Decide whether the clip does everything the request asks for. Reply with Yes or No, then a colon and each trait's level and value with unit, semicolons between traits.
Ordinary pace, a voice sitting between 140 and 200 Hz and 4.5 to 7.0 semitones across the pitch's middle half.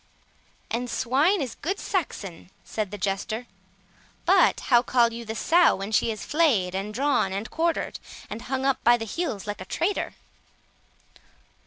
No: average, 160 wpm; high, 235 Hz; wide, 5.6 semitones